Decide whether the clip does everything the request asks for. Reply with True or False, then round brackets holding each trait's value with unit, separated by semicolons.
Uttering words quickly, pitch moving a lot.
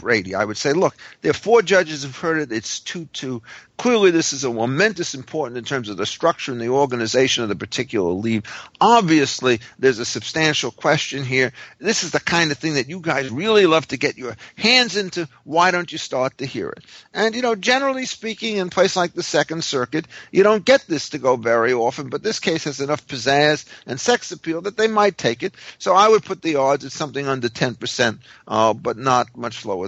True (220 wpm; 6.0 semitones)